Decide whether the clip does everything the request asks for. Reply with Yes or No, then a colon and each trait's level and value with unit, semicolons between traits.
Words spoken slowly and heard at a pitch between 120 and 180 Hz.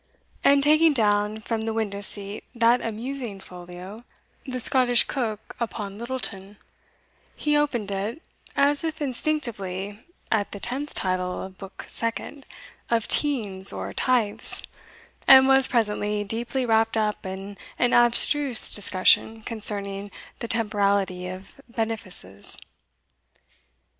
No: slow, 120 wpm; high, 220 Hz